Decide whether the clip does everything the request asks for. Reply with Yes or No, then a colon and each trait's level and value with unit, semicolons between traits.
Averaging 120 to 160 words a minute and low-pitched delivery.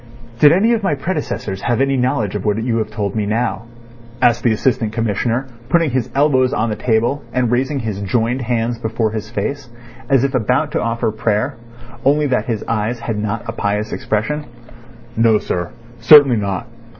No: average, 185 wpm; low, 115 Hz